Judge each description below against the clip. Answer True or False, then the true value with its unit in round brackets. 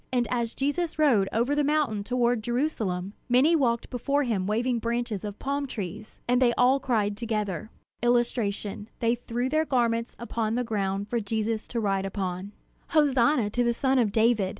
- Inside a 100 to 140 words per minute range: False (175 wpm)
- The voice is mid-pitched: False (235 Hz)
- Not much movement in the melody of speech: False (3.2 semitones)